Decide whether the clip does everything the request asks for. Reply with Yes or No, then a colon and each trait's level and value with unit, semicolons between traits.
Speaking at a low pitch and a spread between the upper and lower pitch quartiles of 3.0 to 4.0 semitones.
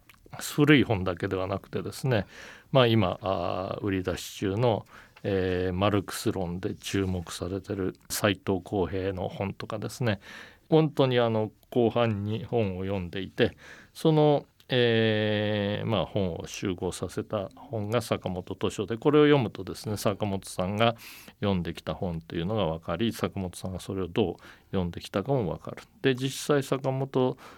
Yes: low, 105 Hz; average, 3.7 semitones